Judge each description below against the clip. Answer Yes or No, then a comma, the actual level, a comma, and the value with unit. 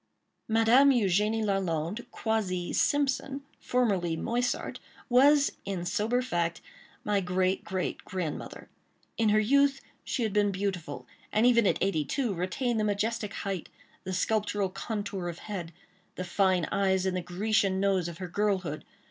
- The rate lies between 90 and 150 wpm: Yes, average, 140 wpm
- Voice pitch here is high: Yes, high, 200 Hz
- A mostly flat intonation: No, average, 3.7 semitones